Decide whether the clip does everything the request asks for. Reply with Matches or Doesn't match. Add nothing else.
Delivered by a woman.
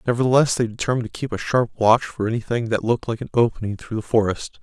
Doesn't match